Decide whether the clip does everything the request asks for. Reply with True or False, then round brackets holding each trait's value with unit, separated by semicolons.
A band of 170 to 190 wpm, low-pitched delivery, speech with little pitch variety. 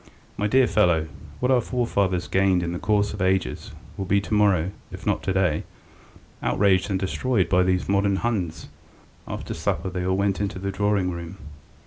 True (185 wpm; 95 Hz; 2.0 semitones)